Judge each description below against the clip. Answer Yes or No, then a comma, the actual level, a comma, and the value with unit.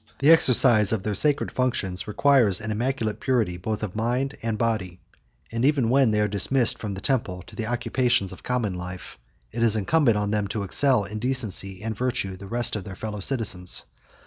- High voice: No, low, 110 Hz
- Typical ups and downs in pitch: Yes, average, 4.0 semitones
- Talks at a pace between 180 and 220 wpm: Yes, average, 200 wpm